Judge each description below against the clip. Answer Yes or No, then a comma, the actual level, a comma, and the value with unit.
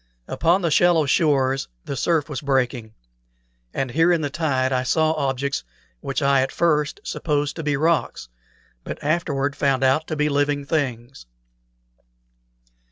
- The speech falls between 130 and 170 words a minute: Yes, average, 150 wpm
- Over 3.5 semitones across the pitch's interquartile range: No, average, 2.8 semitones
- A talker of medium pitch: Yes, medium, 145 Hz